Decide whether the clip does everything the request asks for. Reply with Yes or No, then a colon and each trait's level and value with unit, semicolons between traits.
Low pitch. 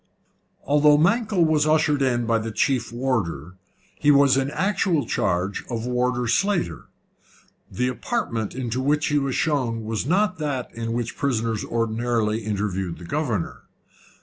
Yes: low, 125 Hz